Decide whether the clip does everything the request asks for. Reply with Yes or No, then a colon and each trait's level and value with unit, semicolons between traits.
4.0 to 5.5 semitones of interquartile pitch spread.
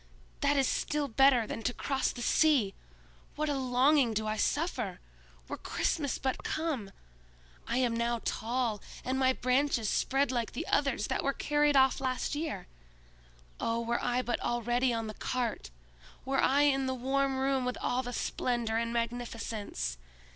No: average, 2.7 semitones